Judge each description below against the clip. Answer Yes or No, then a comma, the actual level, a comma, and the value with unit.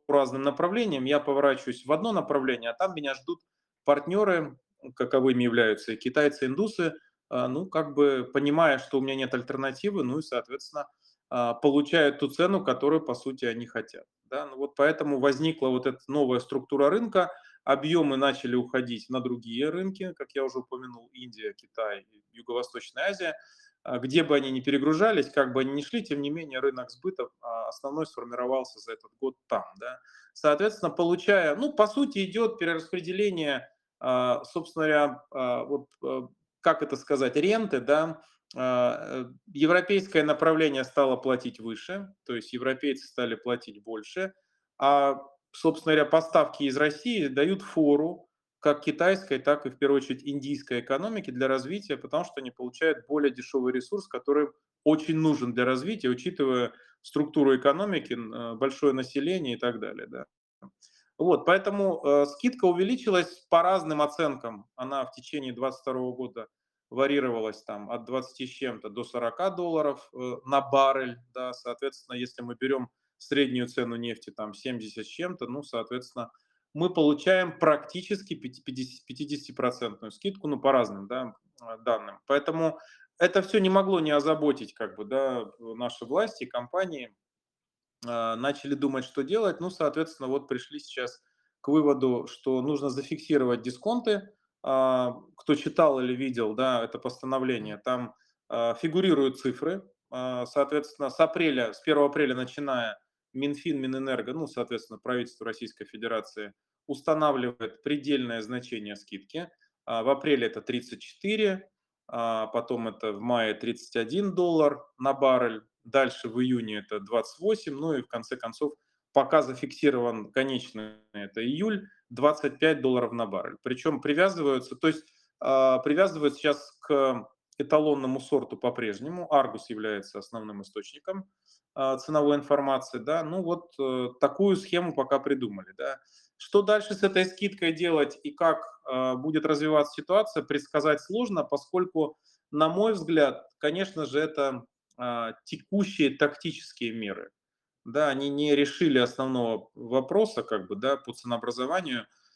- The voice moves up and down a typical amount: Yes, average, 4.2 semitones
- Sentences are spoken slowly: No, average, 135 wpm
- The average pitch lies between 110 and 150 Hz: Yes, medium, 140 Hz